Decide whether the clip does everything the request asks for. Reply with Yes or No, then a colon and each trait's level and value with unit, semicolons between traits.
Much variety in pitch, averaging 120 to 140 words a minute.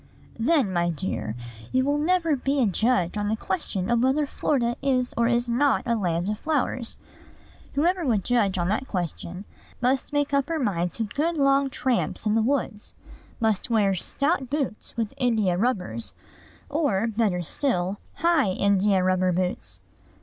No: wide, 6.4 semitones; average, 160 wpm